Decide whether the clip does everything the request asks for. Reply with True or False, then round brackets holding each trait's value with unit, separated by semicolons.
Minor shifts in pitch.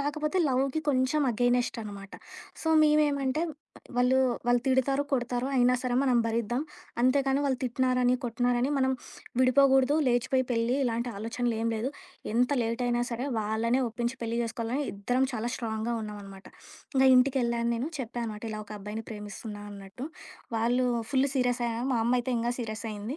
True (2.3 semitones)